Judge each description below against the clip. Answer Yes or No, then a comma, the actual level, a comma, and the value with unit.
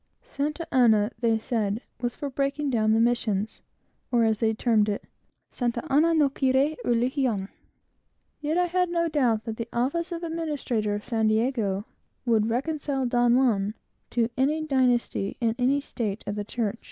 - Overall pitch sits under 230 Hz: No, high, 240 Hz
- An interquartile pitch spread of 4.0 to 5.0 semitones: Yes, average, 4.4 semitones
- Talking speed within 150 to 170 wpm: Yes, average, 165 wpm